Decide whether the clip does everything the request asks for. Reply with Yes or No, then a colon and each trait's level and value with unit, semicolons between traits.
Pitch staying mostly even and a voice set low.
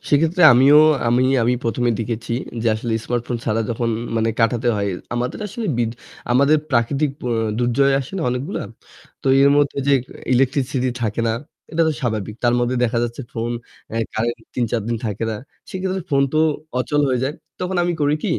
No: average, 3.4 semitones; low, 125 Hz